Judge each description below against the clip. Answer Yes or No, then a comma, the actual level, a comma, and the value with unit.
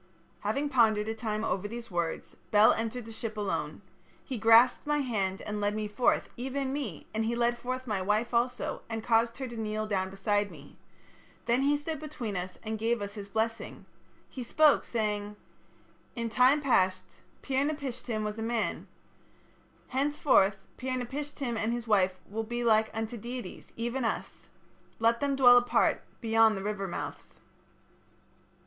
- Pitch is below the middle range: No, high, 225 Hz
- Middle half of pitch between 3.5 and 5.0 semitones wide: No, average, 3.0 semitones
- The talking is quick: No, average, 165 wpm